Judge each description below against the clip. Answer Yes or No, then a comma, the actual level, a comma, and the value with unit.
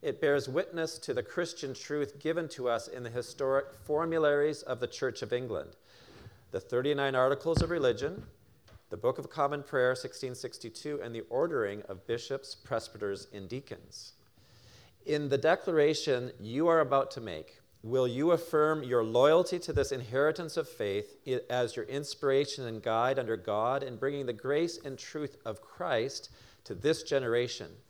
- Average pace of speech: Yes, average, 160 wpm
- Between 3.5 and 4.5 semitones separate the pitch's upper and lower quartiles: Yes, average, 4.0 semitones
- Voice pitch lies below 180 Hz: Yes, low, 135 Hz